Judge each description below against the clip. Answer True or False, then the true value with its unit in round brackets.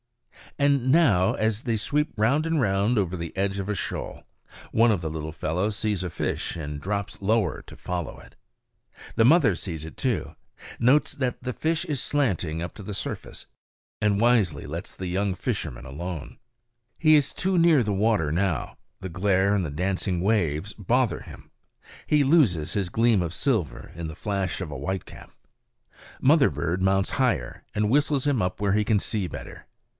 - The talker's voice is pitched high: False (100 Hz)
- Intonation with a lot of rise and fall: True (5.7 semitones)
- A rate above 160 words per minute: True (180 wpm)